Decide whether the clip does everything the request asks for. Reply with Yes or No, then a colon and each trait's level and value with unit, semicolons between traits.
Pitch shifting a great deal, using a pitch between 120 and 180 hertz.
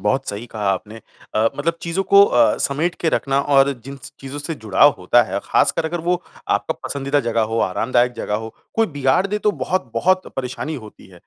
Yes: wide, 6.6 semitones; low, 135 Hz